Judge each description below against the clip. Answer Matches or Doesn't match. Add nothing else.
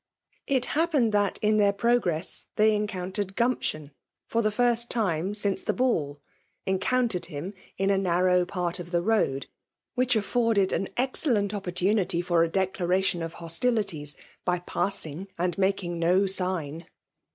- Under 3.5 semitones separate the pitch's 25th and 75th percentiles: Doesn't match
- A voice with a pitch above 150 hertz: Matches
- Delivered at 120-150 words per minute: Matches